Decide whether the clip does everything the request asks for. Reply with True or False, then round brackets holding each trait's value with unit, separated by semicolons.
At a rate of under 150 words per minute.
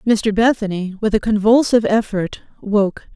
True (135 wpm)